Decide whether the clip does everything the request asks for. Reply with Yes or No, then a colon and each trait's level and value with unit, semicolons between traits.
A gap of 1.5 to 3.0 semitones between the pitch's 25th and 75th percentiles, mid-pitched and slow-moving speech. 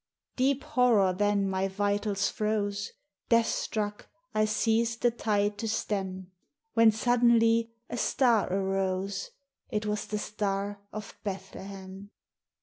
No: narrow, 2.5 semitones; high, 205 Hz; slow, 125 wpm